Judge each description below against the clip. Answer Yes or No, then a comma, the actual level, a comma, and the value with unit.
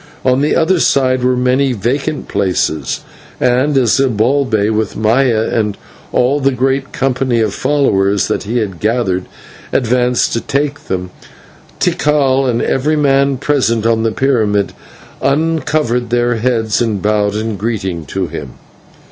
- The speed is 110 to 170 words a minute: Yes, average, 140 wpm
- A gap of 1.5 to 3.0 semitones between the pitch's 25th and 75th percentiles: No, average, 4.1 semitones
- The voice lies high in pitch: No, low, 125 Hz